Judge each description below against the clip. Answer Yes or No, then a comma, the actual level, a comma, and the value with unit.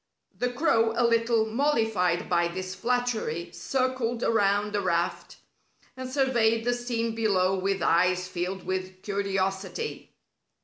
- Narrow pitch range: No, average, 4.4 semitones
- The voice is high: Yes, high, 215 Hz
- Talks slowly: Yes, slow, 125 wpm